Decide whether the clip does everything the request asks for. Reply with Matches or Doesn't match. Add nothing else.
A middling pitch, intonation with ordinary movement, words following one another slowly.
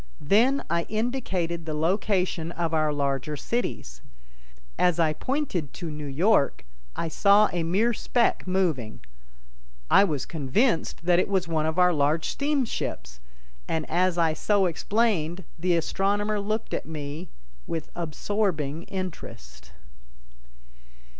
Matches